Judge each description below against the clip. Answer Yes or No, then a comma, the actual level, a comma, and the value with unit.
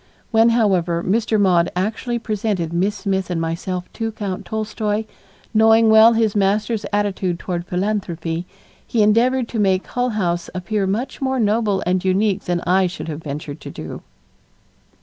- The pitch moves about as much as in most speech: Yes, average, 3.6 semitones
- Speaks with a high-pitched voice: Yes, high, 205 Hz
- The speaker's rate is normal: Yes, average, 155 wpm